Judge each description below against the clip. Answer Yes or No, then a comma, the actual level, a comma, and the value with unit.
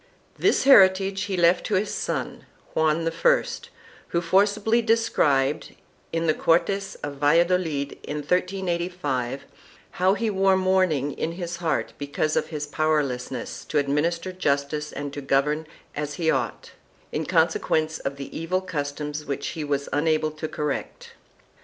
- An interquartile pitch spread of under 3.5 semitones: No, average, 4.2 semitones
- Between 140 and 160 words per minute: Yes, average, 150 wpm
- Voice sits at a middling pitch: Yes, medium, 160 Hz